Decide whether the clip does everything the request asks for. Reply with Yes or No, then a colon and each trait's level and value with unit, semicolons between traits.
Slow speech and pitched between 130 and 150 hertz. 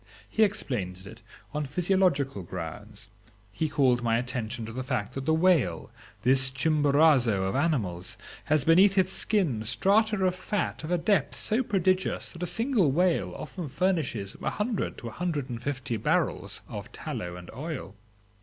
No: average, 165 wpm; medium, 140 Hz